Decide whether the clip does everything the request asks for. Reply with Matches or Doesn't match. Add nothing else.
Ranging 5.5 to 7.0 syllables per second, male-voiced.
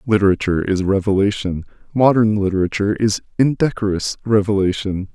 Matches